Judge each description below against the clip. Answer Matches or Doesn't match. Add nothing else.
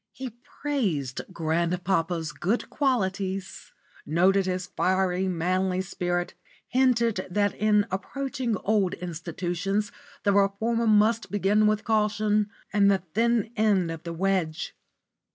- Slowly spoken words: Matches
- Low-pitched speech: Doesn't match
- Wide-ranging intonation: Doesn't match